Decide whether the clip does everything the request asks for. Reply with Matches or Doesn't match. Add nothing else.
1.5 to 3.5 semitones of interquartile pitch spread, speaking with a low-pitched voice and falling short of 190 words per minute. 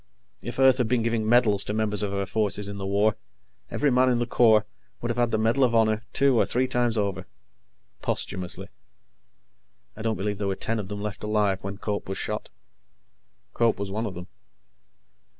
Doesn't match